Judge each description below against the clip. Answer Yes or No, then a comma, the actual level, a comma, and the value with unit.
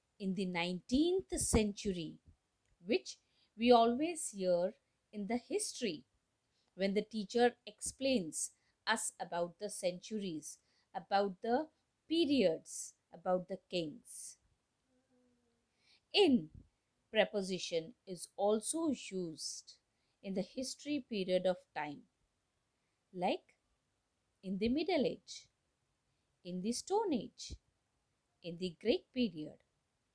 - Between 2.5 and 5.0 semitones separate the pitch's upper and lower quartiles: No, wide, 5.6 semitones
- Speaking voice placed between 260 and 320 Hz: No, high, 205 Hz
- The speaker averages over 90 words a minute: Yes, average, 100 wpm